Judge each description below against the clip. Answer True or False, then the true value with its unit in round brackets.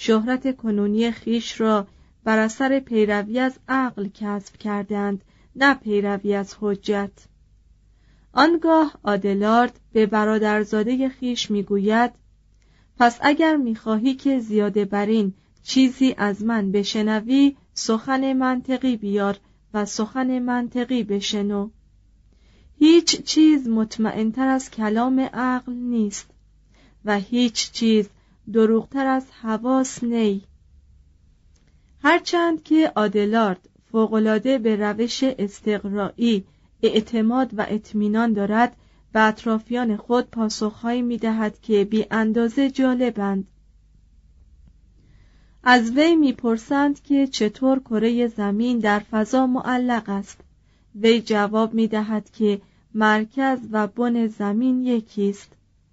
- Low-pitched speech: False (220 Hz)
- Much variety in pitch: False (3.5 semitones)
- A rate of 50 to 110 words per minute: True (105 wpm)